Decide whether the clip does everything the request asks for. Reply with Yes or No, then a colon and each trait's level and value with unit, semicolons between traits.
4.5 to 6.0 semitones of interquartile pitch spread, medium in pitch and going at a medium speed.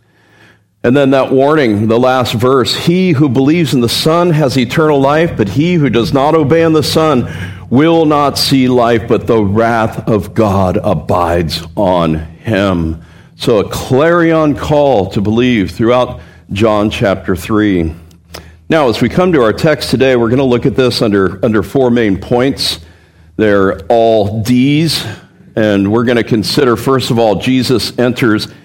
No: average, 5.2 semitones; low, 120 Hz; average, 165 wpm